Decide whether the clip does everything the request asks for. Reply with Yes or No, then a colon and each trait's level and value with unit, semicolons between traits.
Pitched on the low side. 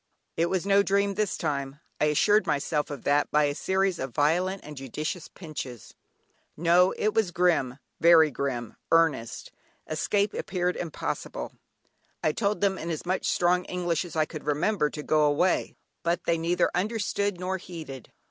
No: medium, 170 Hz